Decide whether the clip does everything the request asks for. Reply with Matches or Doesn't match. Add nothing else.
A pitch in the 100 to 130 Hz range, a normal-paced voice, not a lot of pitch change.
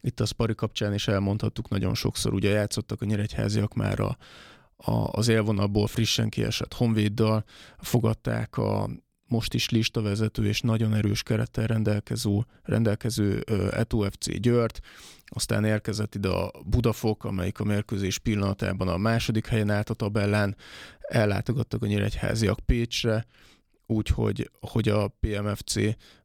Matches